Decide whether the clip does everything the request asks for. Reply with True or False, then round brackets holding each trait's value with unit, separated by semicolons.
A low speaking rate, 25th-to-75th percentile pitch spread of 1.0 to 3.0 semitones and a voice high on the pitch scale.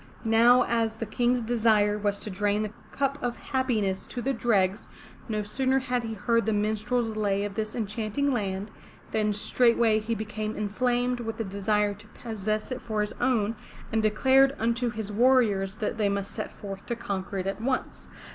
False (185 wpm; 2.7 semitones; 220 Hz)